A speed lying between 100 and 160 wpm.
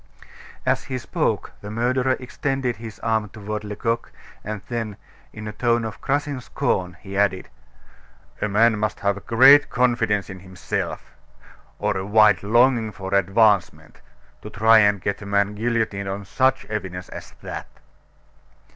Yes: average, 145 wpm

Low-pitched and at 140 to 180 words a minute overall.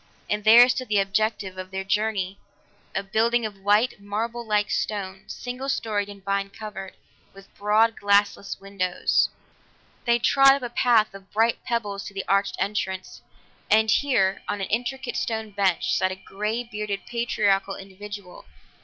No: high, 205 Hz; average, 155 wpm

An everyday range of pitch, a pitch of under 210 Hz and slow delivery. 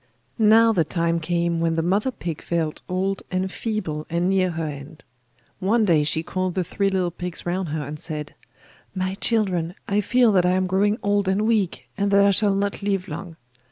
No: average, 3.1 semitones; medium, 185 Hz; average, 200 wpm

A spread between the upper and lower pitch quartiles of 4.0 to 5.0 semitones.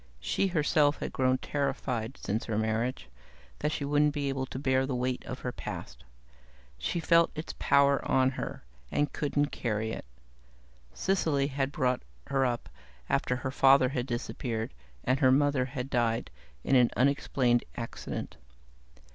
No: narrow, 2.4 semitones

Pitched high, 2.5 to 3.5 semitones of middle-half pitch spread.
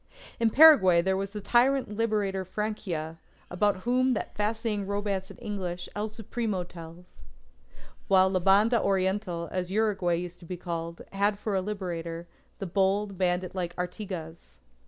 Yes: high, 195 Hz; average, 2.9 semitones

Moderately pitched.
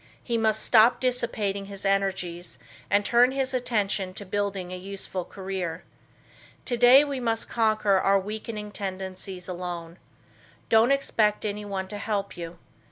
No: high, 200 Hz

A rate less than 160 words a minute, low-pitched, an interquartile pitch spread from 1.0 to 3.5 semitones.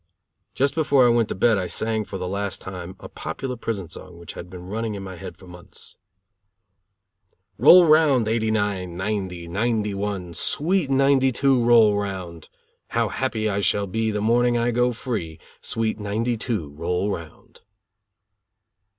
No: average, 150 wpm; low, 105 Hz; average, 4.4 semitones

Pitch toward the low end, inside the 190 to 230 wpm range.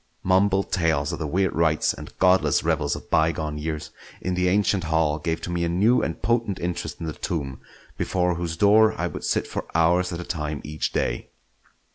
Yes: very low, 85 Hz; average, 200 wpm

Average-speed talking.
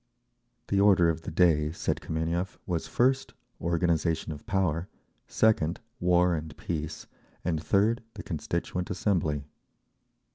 No: slow, 120 wpm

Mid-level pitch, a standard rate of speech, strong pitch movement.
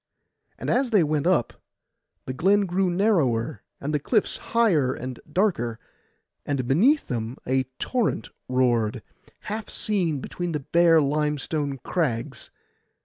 No: medium, 150 Hz; slow, 125 wpm; wide, 6.9 semitones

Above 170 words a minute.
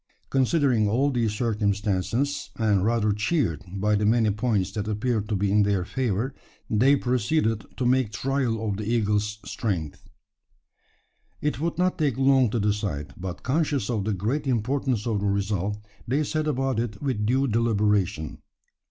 No: average, 160 wpm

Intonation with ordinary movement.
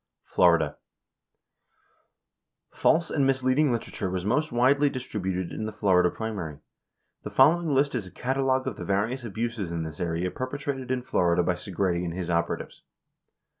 No: wide, 6.6 semitones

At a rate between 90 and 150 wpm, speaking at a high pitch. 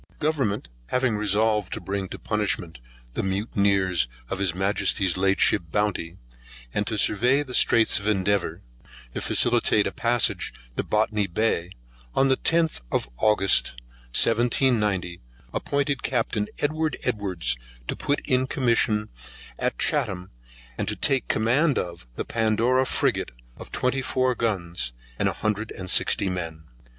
No: average, 140 wpm; low, 105 Hz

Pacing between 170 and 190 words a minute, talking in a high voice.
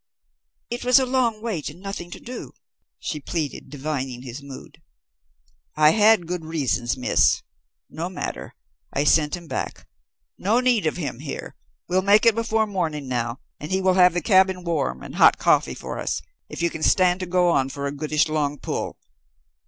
No: average, 185 wpm; medium, 170 Hz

